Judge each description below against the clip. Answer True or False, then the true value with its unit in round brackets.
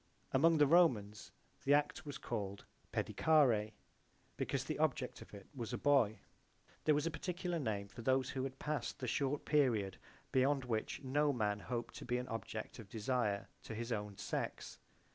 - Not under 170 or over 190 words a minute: True (175 wpm)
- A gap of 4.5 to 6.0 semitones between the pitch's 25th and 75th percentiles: True (5.1 semitones)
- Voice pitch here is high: False (125 Hz)